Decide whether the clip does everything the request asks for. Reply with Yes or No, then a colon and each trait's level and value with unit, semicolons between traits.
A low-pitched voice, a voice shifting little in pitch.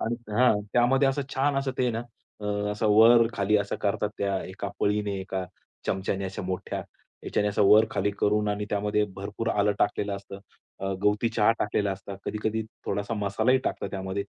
Yes: low, 105 Hz; narrow, 2.0 semitones